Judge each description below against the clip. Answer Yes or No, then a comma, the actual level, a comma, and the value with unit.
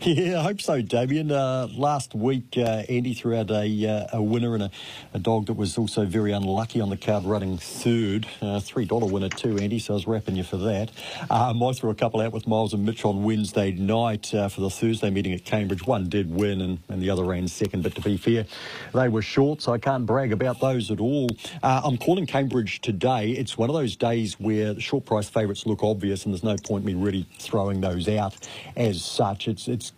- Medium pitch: No, low, 110 Hz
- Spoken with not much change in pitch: No, average, 3.2 semitones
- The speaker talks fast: Yes, fast, 230 wpm